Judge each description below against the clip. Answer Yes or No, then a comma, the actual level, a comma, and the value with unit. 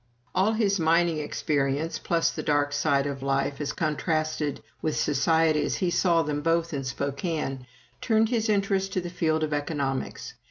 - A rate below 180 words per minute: Yes, average, 165 wpm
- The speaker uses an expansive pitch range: No, average, 3.2 semitones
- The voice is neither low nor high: Yes, medium, 155 Hz